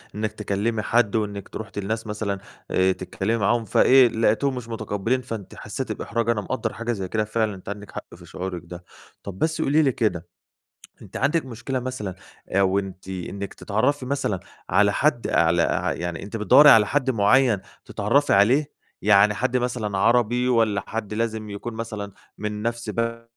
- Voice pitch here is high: No, low, 110 Hz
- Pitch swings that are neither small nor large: Yes, average, 3.0 semitones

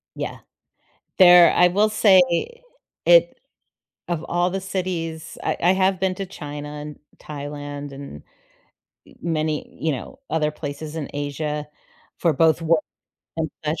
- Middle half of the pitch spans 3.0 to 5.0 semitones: Yes, average, 3.4 semitones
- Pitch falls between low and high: Yes, medium, 160 Hz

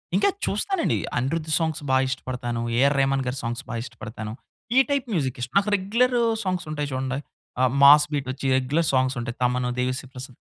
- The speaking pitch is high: No, low, 135 Hz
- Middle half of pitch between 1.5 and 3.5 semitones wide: No, average, 3.9 semitones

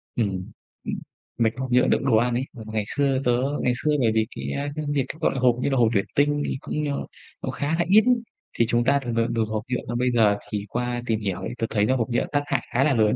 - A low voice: Yes, low, 120 Hz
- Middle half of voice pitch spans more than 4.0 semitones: No, average, 3.5 semitones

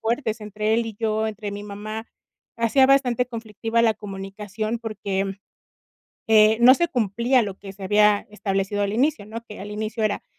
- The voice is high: Yes, high, 215 Hz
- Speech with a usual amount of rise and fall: No, narrow, 2.1 semitones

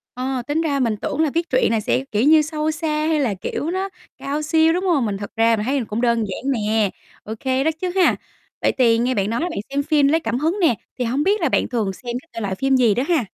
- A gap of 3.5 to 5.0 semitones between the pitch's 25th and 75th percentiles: No, wide, 5.5 semitones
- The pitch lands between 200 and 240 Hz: No, very high, 265 Hz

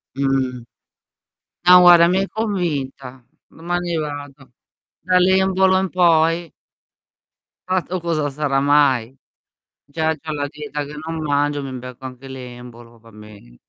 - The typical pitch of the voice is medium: Yes, medium, 145 Hz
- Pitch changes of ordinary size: Yes, average, 4.6 semitones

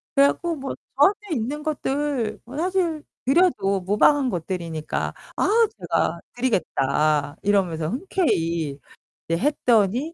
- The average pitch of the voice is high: Yes, high, 245 Hz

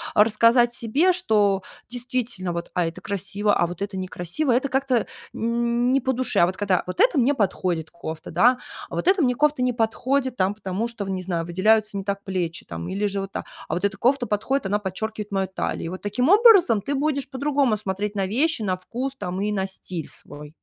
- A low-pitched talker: No, high, 210 Hz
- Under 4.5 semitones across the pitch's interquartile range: No, average, 5.0 semitones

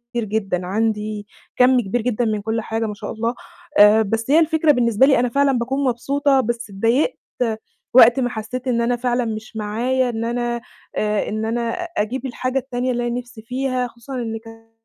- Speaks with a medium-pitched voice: No, high, 235 Hz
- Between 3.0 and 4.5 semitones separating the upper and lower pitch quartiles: No, narrow, 2.4 semitones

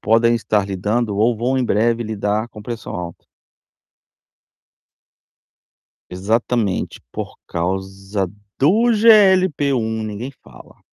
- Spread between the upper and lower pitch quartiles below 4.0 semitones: Yes, average, 3.6 semitones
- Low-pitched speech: Yes, low, 110 Hz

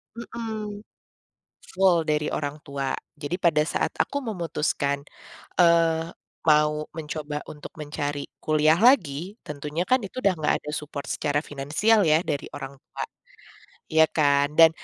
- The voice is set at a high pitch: No, medium, 155 Hz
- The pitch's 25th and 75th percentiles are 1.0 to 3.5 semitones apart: Yes, average, 3.2 semitones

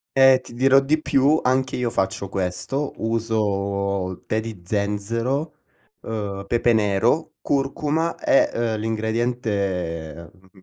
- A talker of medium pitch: No, low, 110 Hz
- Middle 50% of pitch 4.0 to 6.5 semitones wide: Yes, average, 5.1 semitones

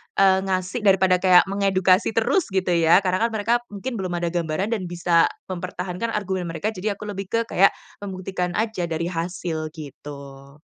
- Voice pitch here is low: No, medium, 185 Hz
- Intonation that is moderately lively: No, narrow, 2.3 semitones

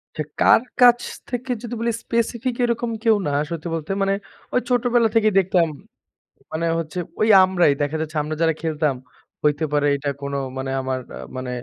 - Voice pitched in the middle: Yes, medium, 170 Hz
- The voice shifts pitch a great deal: Yes, wide, 7.8 semitones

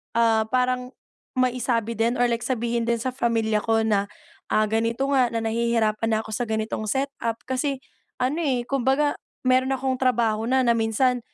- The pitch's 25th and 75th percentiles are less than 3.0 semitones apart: Yes, narrow, 2.4 semitones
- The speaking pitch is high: Yes, high, 235 Hz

